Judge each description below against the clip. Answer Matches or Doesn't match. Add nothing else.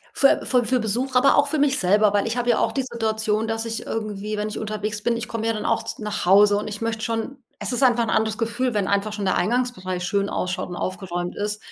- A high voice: Matches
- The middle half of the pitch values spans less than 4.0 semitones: Matches